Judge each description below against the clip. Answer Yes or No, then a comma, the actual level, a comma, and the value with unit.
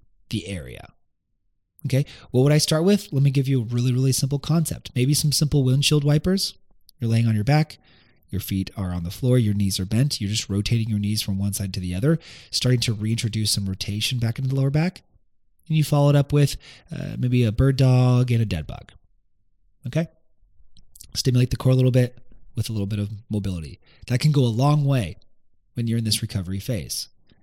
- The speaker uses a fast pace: Yes, fast, 215 wpm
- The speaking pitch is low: Yes, low, 120 Hz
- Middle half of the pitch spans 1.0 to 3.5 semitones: No, average, 5.2 semitones